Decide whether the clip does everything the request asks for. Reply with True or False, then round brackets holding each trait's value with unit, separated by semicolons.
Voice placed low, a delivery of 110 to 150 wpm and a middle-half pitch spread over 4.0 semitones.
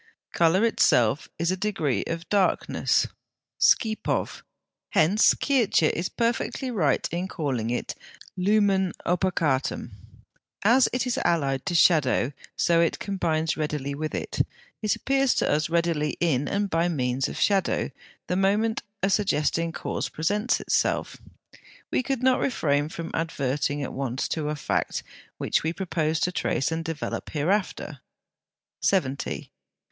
False (170 Hz; 140 wpm; 5.0 semitones)